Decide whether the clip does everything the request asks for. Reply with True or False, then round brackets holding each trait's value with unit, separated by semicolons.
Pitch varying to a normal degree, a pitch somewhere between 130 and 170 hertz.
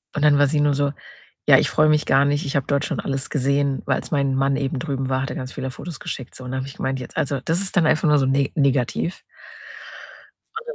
False (1.8 semitones; 140 Hz)